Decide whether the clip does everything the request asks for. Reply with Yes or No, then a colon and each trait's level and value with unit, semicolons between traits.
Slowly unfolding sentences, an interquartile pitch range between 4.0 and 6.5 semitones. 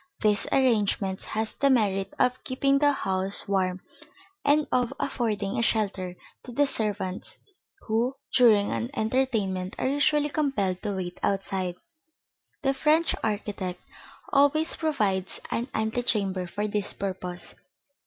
Yes: slow, 125 wpm; wide, 5.5 semitones